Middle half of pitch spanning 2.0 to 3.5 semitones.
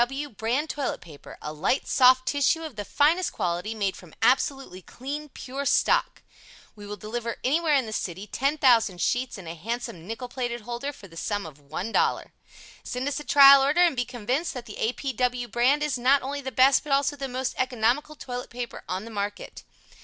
No: average, 4.5 semitones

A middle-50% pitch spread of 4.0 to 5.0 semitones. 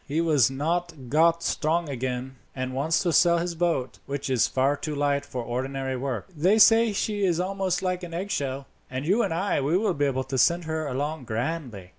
Yes: average, 4.6 semitones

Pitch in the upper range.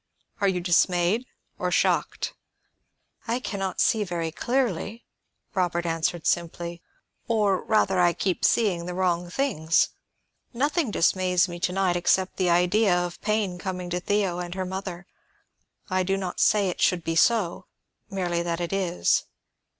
No: medium, 180 Hz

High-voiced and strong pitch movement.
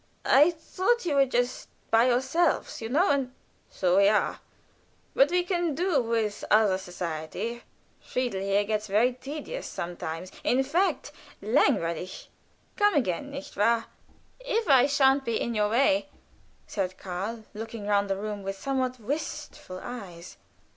Yes: high, 235 Hz; wide, 5.9 semitones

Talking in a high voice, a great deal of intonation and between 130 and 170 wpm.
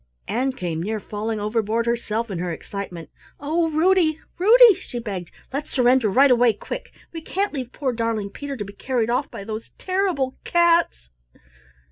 Yes: high, 240 Hz; wide, 6.3 semitones; average, 165 wpm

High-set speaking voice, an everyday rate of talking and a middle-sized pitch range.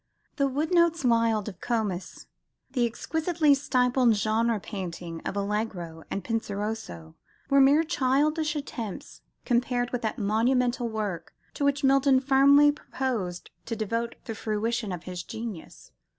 No: high, 235 Hz; slow, 130 wpm; average, 4.7 semitones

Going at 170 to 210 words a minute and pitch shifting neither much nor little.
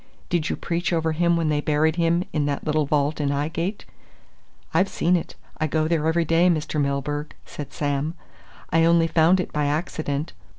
No: average, 185 wpm; narrow, 2.2 semitones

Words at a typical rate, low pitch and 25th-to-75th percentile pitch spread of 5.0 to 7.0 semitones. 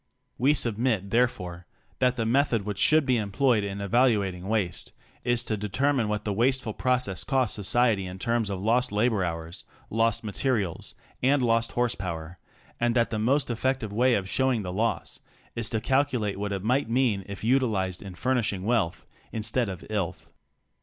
No: average, 180 wpm; low, 110 Hz; average, 4.0 semitones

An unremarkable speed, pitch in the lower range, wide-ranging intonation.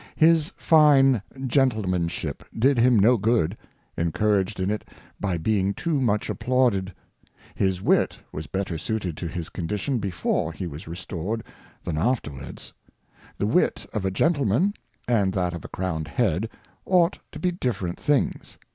Yes: average, 145 wpm; low, 100 Hz; wide, 6.2 semitones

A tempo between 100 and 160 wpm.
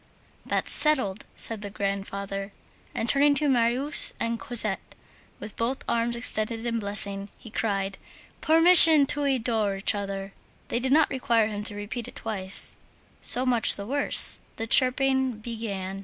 Yes: average, 150 wpm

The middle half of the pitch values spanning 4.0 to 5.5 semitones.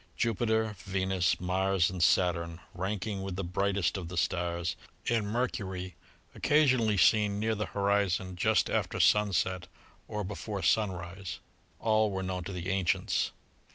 No: narrow, 2.6 semitones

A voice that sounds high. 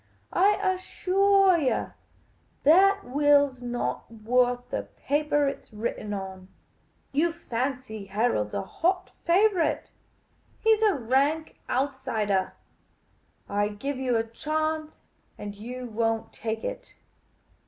Yes: very high, 265 Hz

